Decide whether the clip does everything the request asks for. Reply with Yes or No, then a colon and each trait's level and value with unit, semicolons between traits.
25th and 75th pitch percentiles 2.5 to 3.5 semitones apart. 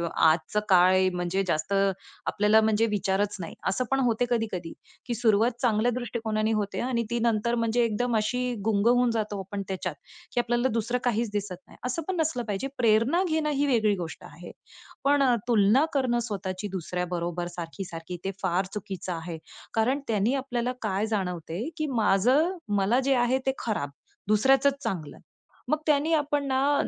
No: average, 4.4 semitones